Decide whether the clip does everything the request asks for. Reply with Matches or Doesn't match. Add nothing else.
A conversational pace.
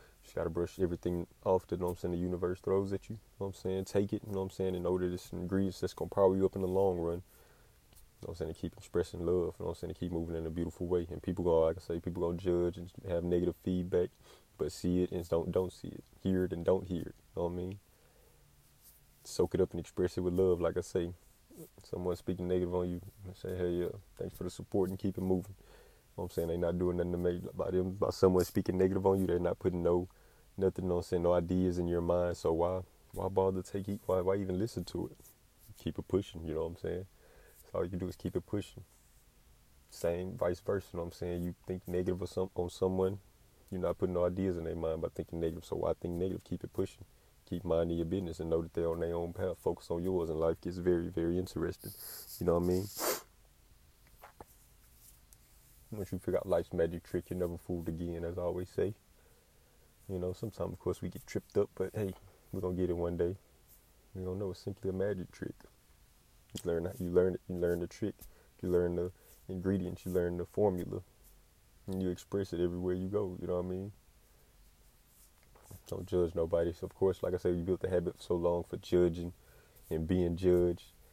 Doesn't match